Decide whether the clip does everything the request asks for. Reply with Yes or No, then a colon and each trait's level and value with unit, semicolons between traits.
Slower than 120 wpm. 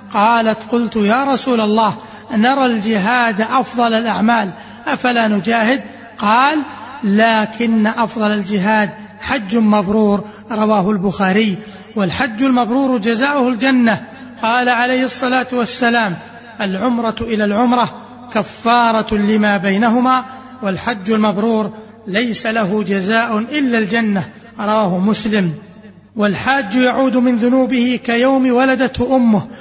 Yes: average, 100 wpm